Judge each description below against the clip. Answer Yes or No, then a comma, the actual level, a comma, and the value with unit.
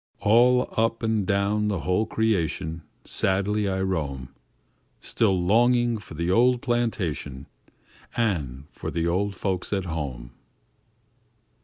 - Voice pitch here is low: Yes, low, 100 Hz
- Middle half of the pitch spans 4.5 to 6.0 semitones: Yes, average, 5.1 semitones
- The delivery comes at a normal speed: No, slow, 120 wpm